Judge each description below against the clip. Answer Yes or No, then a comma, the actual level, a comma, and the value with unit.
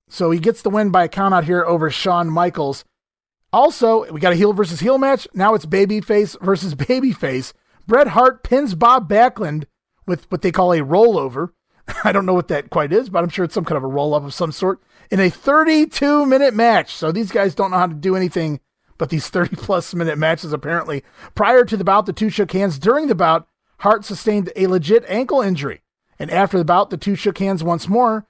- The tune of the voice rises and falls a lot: No, average, 4.2 semitones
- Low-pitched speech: No, high, 195 Hz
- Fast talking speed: Yes, fast, 220 wpm